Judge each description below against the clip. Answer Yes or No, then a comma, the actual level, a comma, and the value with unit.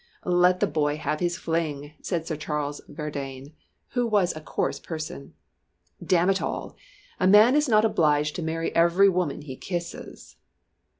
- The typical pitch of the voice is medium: Yes, medium, 165 Hz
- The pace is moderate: Yes, average, 160 wpm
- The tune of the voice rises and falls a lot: No, average, 3.5 semitones